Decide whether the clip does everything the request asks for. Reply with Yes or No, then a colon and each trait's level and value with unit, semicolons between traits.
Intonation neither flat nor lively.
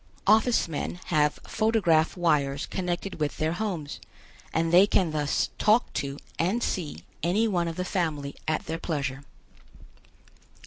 Yes: average, 4.1 semitones